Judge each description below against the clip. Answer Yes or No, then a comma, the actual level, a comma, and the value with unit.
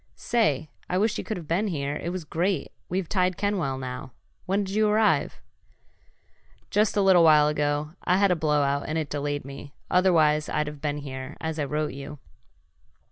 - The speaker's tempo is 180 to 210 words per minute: Yes, average, 185 wpm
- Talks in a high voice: No, medium, 155 Hz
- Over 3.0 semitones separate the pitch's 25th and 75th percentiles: Yes, average, 4.3 semitones